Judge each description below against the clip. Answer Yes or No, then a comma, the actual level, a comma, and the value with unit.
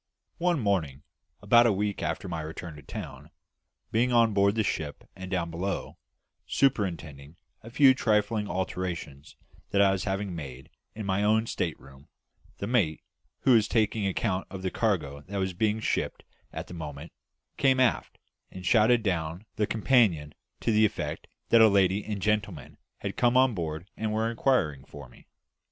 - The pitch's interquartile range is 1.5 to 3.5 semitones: No, average, 4.8 semitones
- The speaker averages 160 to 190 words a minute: Yes, average, 170 wpm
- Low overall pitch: Yes, low, 100 Hz